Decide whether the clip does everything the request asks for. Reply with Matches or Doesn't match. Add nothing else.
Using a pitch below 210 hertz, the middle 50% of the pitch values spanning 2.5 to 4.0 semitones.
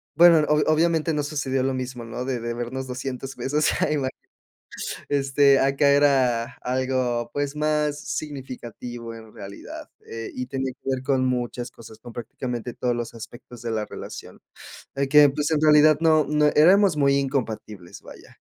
Matches